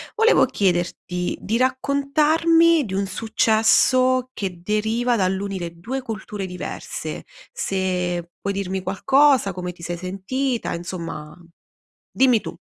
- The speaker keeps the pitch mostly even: No, wide, 6.0 semitones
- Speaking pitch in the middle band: No, high, 200 Hz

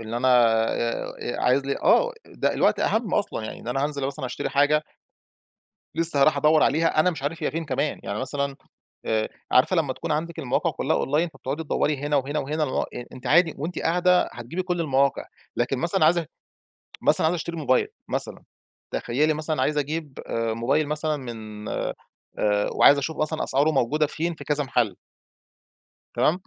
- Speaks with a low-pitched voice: No, medium, 145 Hz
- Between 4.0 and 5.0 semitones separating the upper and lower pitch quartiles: No, average, 3.4 semitones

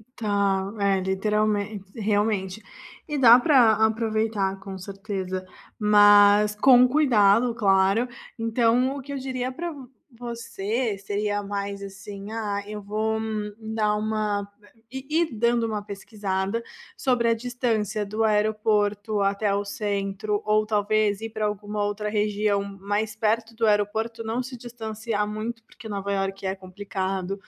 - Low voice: No, high, 210 Hz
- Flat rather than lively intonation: Yes, narrow, 1.9 semitones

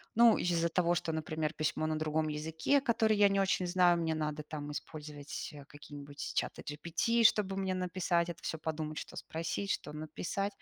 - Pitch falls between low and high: Yes, medium, 160 Hz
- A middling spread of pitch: Yes, average, 3.4 semitones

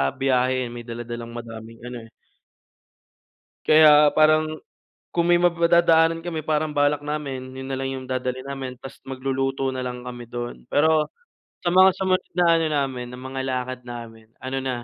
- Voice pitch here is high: No, low, 135 Hz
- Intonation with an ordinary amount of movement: Yes, average, 3.7 semitones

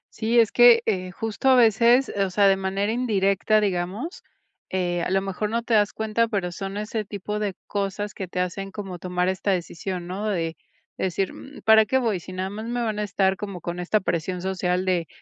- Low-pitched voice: No, high, 195 Hz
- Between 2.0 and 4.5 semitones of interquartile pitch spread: Yes, average, 2.9 semitones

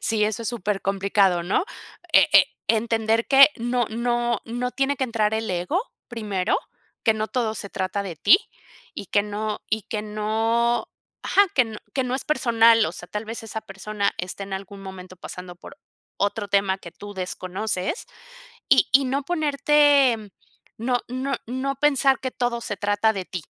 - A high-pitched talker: Yes, high, 220 Hz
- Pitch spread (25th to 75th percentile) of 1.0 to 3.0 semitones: No, average, 3.7 semitones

